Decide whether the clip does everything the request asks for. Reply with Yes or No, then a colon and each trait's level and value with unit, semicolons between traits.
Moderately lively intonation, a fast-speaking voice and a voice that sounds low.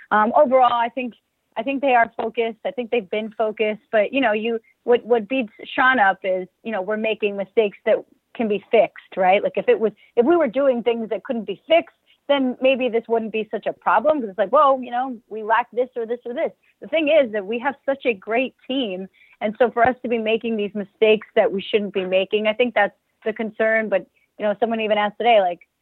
No: average, 3.0 semitones; fast, 245 wpm; high, 230 Hz